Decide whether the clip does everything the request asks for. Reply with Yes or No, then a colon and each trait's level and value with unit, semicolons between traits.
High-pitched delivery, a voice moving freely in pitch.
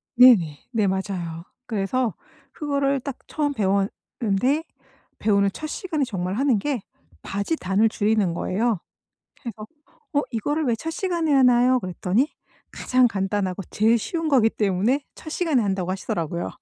Yes: high, 225 Hz; wide, 6.1 semitones